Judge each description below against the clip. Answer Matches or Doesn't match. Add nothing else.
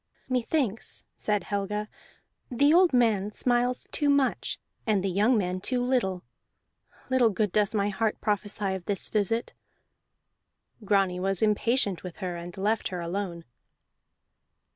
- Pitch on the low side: Doesn't match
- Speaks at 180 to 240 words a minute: Doesn't match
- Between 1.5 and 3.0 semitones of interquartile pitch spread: Doesn't match